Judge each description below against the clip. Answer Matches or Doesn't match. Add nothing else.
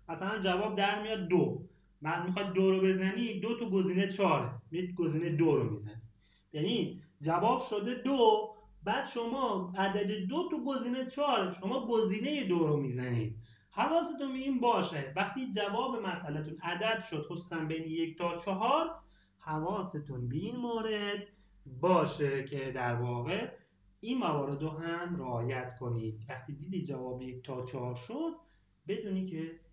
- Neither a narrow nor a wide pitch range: Doesn't match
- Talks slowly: Doesn't match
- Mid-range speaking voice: Matches